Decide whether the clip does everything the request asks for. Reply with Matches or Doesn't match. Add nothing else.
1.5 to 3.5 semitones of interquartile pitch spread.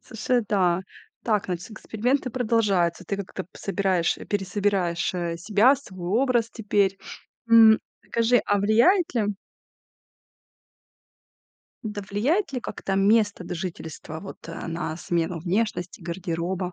Doesn't match